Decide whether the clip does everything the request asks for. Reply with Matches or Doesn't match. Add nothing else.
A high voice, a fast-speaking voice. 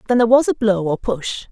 Matches